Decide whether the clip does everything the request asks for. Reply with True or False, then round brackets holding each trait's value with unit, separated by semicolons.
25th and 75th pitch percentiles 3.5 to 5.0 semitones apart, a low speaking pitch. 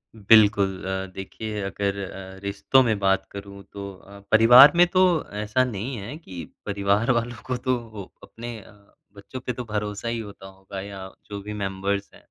False (2.9 semitones; 100 Hz)